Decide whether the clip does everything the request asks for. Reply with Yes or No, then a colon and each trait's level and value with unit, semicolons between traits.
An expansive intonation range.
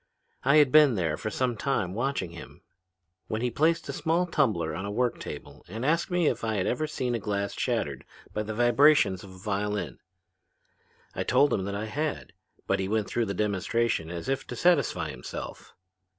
Yes: wide, 5.9 semitones